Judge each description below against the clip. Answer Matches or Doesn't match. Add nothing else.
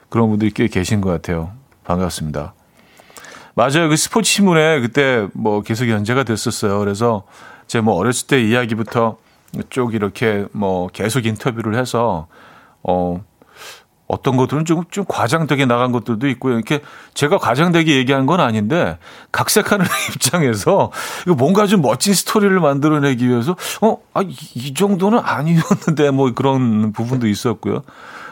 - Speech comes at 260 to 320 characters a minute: Matches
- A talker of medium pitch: Doesn't match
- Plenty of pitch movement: Matches